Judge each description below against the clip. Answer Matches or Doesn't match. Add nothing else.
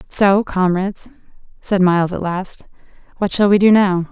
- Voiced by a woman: Matches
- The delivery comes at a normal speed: Matches